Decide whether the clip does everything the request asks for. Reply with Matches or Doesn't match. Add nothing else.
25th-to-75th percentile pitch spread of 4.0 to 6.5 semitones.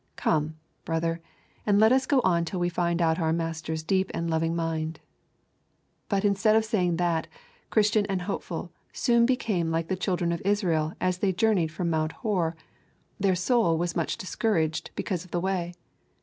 Doesn't match